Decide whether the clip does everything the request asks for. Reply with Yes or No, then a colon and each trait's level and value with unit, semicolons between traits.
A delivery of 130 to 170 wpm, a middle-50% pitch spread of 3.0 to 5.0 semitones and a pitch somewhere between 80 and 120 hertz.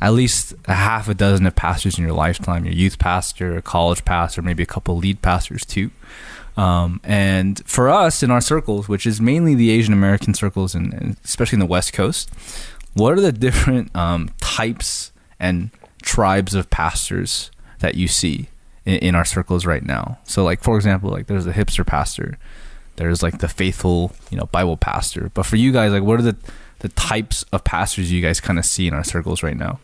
No: fast, 205 wpm; average, 3.4 semitones; very low, 95 Hz